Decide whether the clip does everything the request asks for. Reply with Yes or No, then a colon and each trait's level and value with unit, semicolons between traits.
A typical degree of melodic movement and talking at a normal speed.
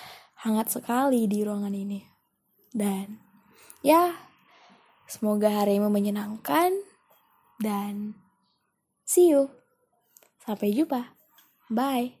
No: average, 4.4 semitones; slow, 80 wpm